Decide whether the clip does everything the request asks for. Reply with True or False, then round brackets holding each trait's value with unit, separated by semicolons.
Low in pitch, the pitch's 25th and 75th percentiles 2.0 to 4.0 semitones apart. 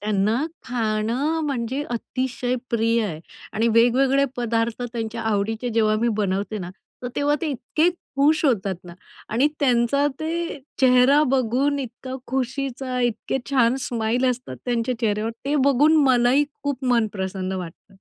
False (245 Hz; 3.4 semitones)